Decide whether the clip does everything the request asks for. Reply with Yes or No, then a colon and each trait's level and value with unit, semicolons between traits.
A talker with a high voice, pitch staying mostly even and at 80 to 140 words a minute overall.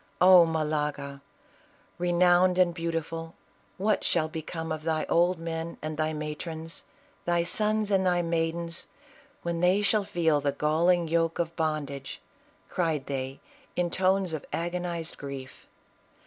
No: medium, 165 Hz; narrow, 2.2 semitones; slow, 135 wpm